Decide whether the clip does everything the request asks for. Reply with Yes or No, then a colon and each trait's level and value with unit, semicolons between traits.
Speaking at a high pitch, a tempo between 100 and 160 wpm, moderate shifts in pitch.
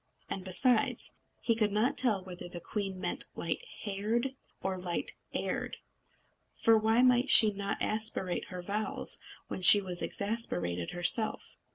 Yes: high, 205 Hz; average, 145 wpm; average, 3.5 semitones